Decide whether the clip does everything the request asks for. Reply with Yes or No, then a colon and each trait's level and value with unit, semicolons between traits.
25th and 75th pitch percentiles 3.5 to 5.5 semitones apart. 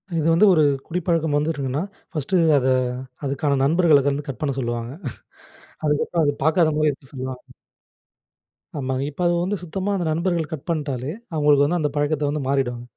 No: average, 3.1 semitones